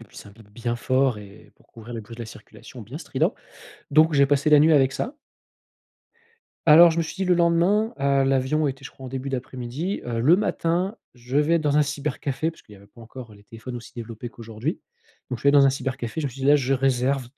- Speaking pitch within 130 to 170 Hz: Yes, low, 135 Hz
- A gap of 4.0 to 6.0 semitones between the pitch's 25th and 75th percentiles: Yes, average, 4.3 semitones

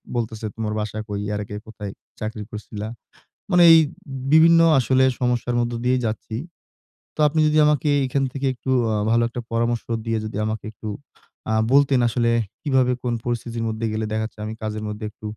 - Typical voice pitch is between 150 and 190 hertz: No, low, 115 Hz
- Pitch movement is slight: No, average, 3.0 semitones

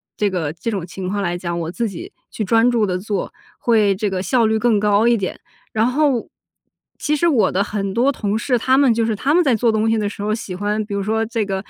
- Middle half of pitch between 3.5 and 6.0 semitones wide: No, average, 2.9 semitones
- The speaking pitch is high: Yes, high, 215 Hz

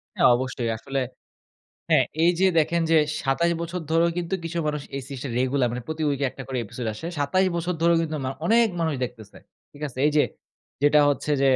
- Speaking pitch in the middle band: Yes, medium, 150 Hz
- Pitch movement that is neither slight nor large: Yes, average, 4.1 semitones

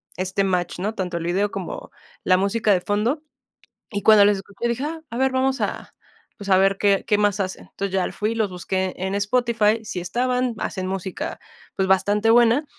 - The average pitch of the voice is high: Yes, high, 205 Hz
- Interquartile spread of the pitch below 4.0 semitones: Yes, average, 3.6 semitones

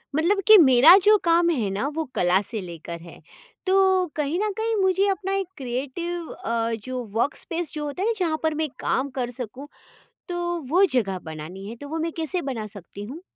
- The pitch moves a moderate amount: No, wide, 7.4 semitones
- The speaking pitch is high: Yes, very high, 300 Hz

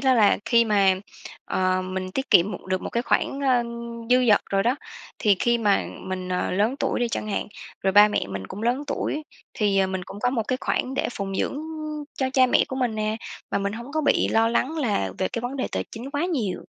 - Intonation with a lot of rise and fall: No, average, 5.0 semitones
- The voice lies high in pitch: Yes, high, 225 Hz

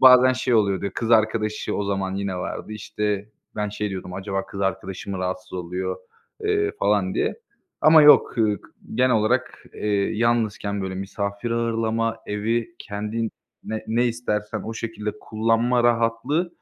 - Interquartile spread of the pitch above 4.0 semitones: No, average, 2.7 semitones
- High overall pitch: No, low, 110 Hz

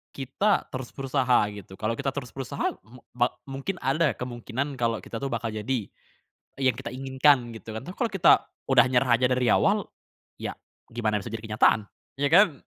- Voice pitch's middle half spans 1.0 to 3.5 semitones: Yes, average, 3.0 semitones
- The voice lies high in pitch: No, low, 125 Hz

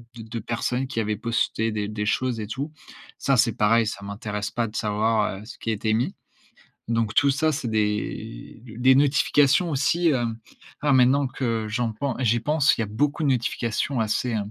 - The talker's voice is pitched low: Yes, low, 115 Hz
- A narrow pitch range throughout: No, average, 3.6 semitones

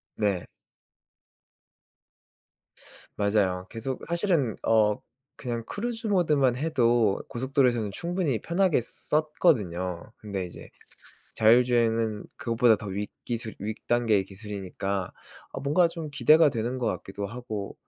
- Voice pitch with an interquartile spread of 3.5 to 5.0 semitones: No, wide, 5.5 semitones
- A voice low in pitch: Yes, low, 115 Hz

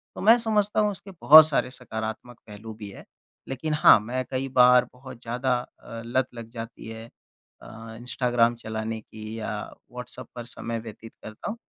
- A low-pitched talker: Yes, low, 120 Hz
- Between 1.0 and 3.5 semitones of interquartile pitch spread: Yes, average, 2.7 semitones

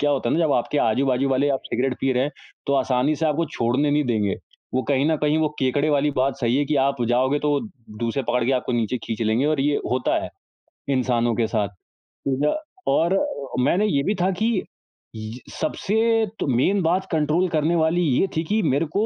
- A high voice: No, medium, 140 Hz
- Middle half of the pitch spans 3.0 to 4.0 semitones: Yes, average, 3.7 semitones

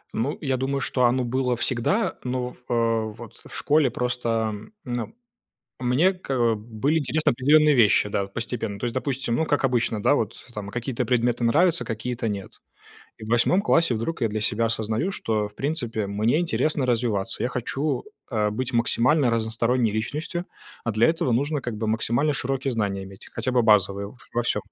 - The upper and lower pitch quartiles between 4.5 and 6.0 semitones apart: No, average, 3.3 semitones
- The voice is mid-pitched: No, low, 120 Hz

